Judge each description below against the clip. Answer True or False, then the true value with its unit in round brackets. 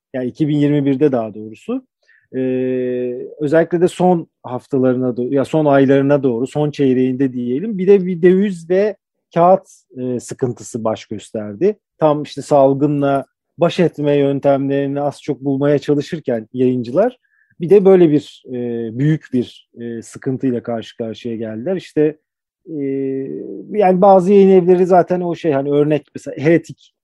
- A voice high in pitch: False (140 Hz)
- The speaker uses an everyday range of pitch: True (4.8 semitones)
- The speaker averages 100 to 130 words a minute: False (140 wpm)